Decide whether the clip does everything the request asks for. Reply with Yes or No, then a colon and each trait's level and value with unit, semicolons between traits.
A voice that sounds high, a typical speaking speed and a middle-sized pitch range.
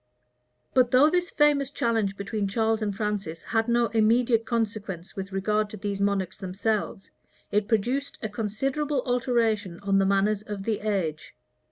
Yes: high, 215 Hz; average, 155 wpm; average, 3.0 semitones